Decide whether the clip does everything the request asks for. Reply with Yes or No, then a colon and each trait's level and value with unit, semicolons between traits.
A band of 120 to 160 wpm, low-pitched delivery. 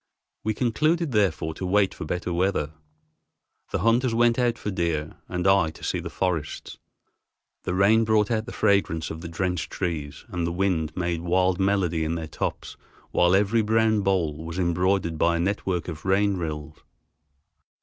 No: average, 170 wpm; very low, 90 Hz